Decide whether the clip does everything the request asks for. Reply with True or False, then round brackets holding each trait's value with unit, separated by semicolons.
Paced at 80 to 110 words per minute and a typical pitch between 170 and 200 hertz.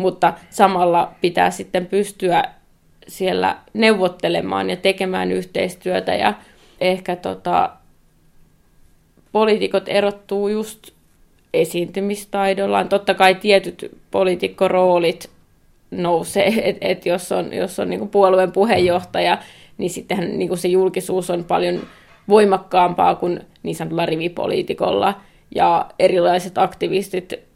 True (100 wpm; 185 Hz)